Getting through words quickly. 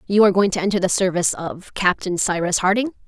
Yes: fast, 215 wpm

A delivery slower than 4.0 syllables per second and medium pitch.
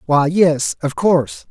Yes: 3.8 syllables/s; medium, 150 Hz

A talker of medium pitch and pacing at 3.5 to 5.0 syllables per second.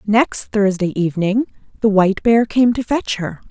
No: high, 210 Hz; 4.8 syllables/s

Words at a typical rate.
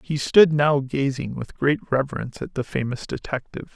Yes: average, 175 wpm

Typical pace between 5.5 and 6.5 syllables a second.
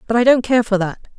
No: 7.0 syllables/s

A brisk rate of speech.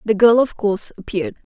No: average, 190 wpm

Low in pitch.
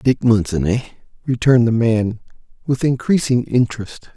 Yes: low, 120 Hz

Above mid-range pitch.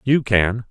No: low, 115 Hz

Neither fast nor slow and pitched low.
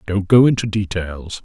Yes: average, 165 wpm; low, 100 Hz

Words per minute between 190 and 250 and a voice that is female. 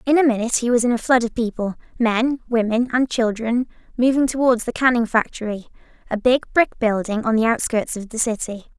Yes: average, 200 wpm; female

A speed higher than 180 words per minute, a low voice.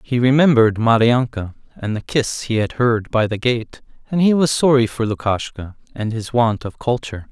Yes: average, 190 wpm; low, 120 Hz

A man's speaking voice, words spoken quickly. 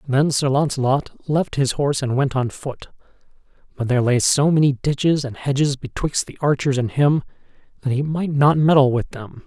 No: male; average, 190 wpm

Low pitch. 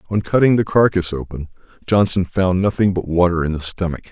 Yes: very low, 90 Hz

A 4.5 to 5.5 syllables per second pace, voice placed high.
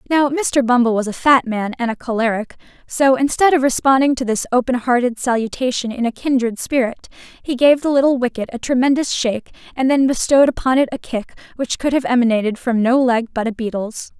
No: 5.8 syllables/s; very high, 250 Hz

